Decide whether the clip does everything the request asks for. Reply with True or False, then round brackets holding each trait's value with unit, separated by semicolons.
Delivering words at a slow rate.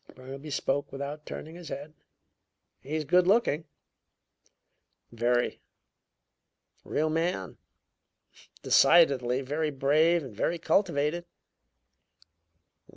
True (90 wpm)